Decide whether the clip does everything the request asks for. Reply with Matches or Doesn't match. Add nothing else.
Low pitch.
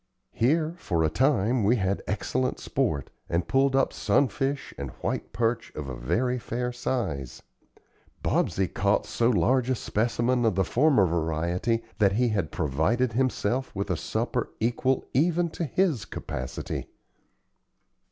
Matches